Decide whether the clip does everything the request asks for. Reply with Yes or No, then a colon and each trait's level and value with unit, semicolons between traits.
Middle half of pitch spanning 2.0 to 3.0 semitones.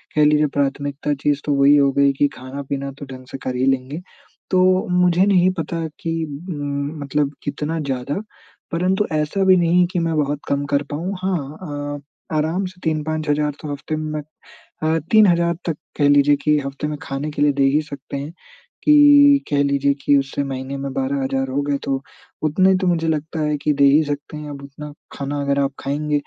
Yes: narrow, 2.4 semitones